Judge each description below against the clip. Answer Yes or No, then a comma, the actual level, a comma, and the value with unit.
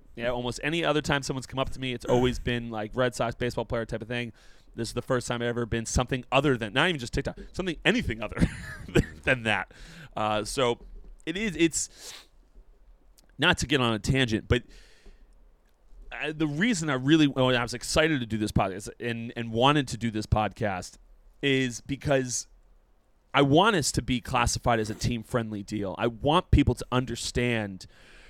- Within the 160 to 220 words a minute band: Yes, average, 195 wpm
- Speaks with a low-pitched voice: Yes, low, 120 Hz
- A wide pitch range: No, average, 3.2 semitones